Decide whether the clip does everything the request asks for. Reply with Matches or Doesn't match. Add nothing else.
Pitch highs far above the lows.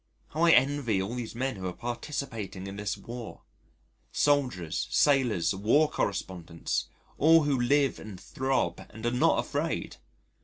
Matches